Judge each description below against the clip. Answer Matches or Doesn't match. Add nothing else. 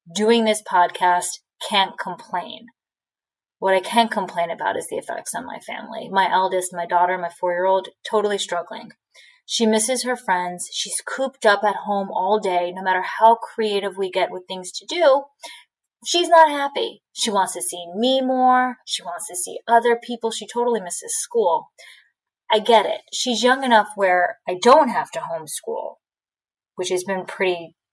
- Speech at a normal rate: Matches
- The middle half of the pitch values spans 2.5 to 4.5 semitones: Doesn't match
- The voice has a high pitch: Matches